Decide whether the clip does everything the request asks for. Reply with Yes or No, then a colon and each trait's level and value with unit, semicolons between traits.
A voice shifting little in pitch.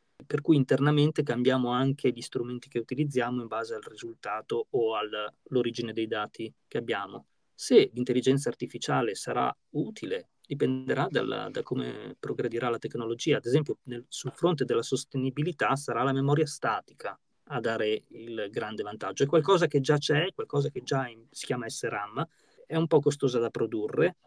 No: average, 4.4 semitones